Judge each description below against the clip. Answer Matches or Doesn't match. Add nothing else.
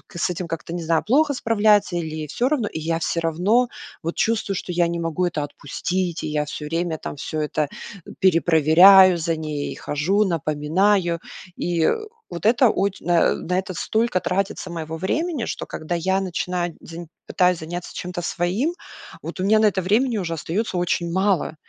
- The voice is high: Doesn't match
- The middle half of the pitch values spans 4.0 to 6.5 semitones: Doesn't match